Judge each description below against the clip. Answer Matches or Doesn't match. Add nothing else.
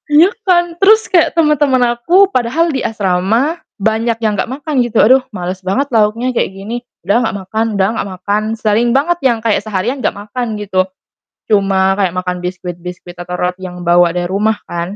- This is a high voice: Matches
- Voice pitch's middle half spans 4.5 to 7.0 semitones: Matches